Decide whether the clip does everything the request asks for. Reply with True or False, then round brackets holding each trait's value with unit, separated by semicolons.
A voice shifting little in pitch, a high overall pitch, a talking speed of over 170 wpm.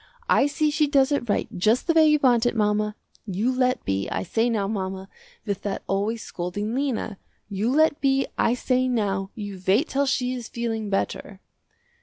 False (4.7 semitones; 225 Hz; 190 wpm)